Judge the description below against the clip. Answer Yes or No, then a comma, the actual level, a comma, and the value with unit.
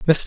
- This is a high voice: No, medium, 160 Hz